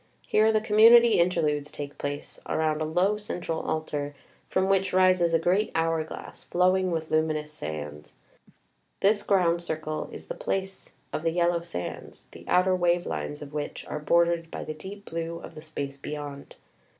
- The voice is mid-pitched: Yes, medium, 165 Hz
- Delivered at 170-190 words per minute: Yes, average, 175 wpm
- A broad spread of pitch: No, average, 3.4 semitones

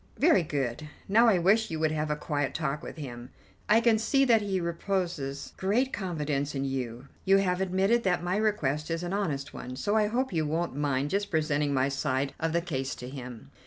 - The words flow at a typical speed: No, fast, 210 wpm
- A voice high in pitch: No, medium, 165 Hz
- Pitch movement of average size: No, wide, 5.9 semitones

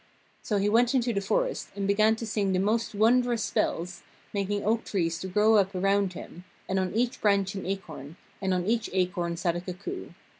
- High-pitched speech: Yes, high, 200 Hz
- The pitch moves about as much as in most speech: Yes, average, 3.2 semitones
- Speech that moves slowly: No, average, 200 wpm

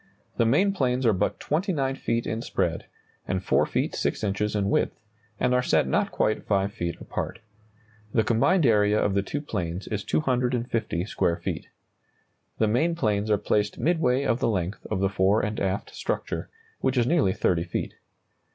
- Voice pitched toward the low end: Yes, low, 110 Hz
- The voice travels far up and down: No, average, 4.3 semitones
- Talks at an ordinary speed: Yes, average, 180 wpm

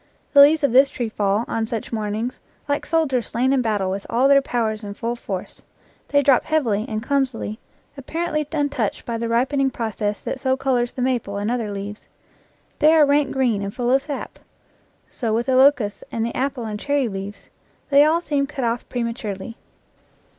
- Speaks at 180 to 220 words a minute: Yes, average, 190 wpm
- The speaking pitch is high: Yes, high, 245 Hz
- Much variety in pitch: No, average, 4.2 semitones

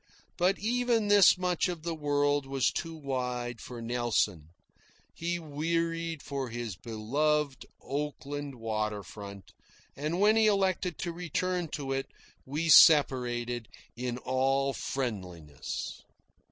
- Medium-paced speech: No, slow, 120 wpm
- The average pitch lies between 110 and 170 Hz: Yes, medium, 140 Hz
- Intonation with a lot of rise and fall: Yes, wide, 5.7 semitones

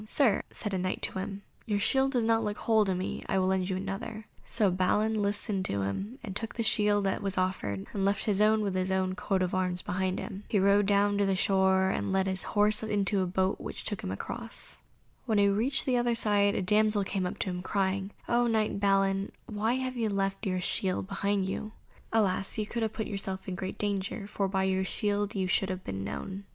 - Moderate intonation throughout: No, narrow, 2.0 semitones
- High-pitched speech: Yes, high, 200 Hz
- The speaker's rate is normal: No, fast, 230 wpm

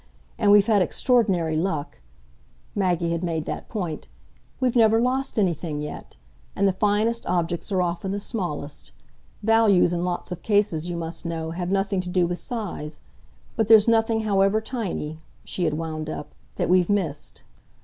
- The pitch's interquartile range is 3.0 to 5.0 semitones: Yes, average, 4.2 semitones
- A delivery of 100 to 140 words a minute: No, average, 165 wpm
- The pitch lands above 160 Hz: Yes, medium, 185 Hz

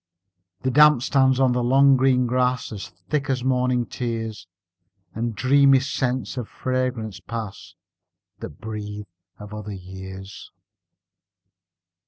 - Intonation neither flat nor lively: Yes, average, 3.7 semitones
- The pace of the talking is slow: Yes, slow, 120 wpm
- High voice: No, low, 125 Hz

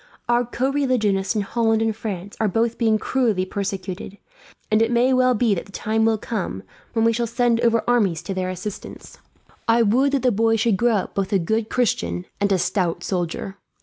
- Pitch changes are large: No, average, 3.4 semitones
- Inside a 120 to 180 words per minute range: No, fast, 205 wpm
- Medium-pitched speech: No, high, 220 Hz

